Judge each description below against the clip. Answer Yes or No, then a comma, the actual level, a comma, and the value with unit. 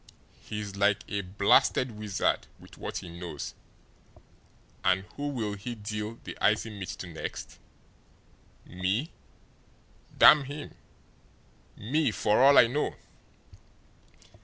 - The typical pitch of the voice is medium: No, low, 105 Hz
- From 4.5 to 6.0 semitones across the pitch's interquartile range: No, average, 3.9 semitones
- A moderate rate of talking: No, slow, 110 wpm